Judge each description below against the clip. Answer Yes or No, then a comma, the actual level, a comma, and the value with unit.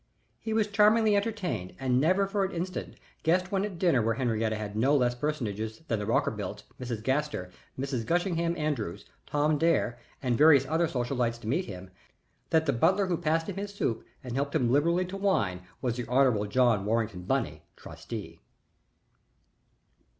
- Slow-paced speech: No, average, 170 wpm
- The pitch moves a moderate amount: No, wide, 7.2 semitones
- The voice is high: No, medium, 140 Hz